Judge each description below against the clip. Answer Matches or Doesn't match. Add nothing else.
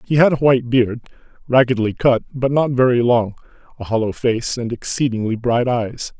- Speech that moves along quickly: Doesn't match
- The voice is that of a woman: Doesn't match